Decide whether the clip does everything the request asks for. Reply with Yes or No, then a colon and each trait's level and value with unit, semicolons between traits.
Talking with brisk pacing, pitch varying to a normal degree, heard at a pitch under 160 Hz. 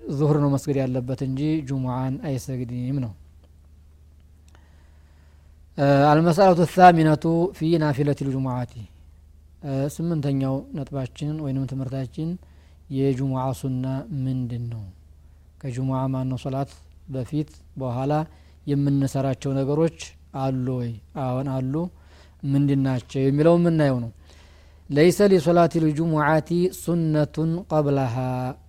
No: average, 95 wpm; average, 4.9 semitones; low, 135 Hz